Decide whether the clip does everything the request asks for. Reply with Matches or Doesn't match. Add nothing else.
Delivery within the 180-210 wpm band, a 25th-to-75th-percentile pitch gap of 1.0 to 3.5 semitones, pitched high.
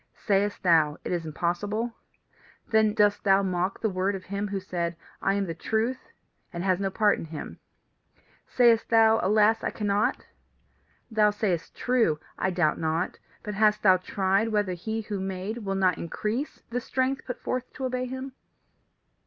Doesn't match